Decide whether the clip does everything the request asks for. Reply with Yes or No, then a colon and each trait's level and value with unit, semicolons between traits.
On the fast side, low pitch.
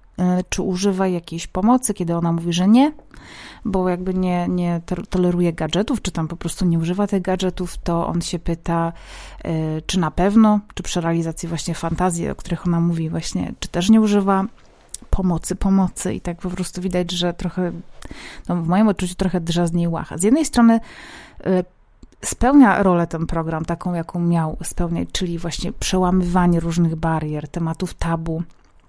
No: fast, 165 wpm; medium, 175 Hz